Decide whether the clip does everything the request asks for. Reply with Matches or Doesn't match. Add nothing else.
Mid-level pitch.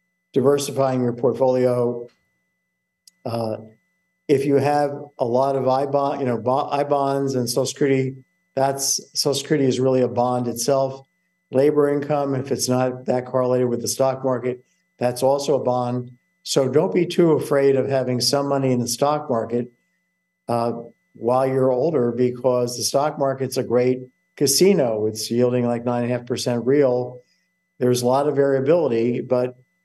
Doesn't match